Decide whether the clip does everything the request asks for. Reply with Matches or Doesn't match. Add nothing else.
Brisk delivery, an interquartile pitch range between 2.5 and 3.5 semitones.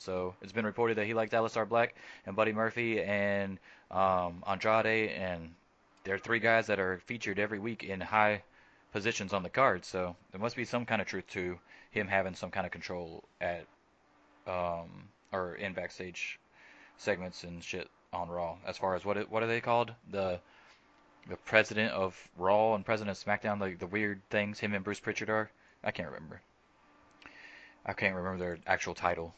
Doesn't match